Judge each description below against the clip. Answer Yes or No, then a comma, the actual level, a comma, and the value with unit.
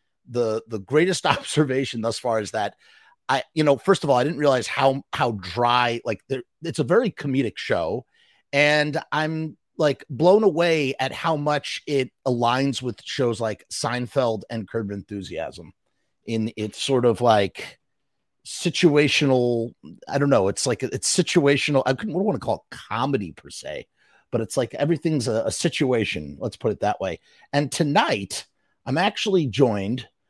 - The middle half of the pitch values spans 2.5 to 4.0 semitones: No, average, 4.5 semitones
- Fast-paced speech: No, average, 165 wpm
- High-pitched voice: No, low, 135 Hz